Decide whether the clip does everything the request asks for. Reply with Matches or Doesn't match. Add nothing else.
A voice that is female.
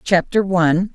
Matches